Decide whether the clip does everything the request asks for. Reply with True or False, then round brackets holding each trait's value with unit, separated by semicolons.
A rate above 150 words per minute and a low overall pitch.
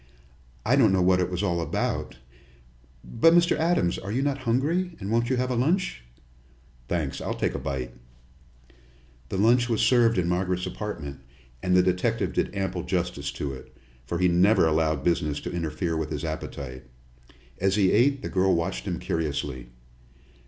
True (175 wpm; 90 Hz)